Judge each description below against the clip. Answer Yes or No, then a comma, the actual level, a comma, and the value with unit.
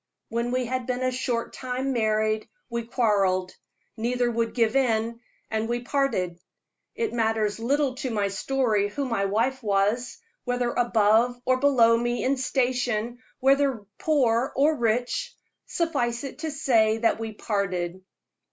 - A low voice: No, high, 240 Hz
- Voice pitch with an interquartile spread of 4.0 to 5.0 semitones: No, average, 2.8 semitones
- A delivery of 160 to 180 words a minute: No, average, 145 wpm